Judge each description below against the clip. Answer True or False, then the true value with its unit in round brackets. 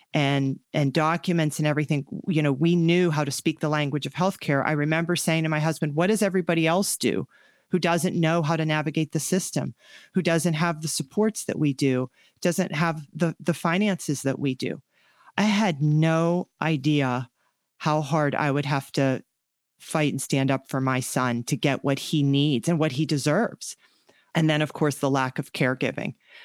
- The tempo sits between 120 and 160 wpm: False (195 wpm)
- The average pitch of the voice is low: False (155 Hz)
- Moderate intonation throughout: True (3.2 semitones)